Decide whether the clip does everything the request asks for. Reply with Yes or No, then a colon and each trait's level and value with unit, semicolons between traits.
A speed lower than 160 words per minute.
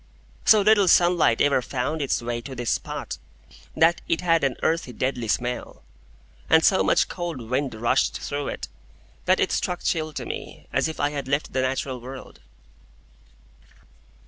No: average, 165 wpm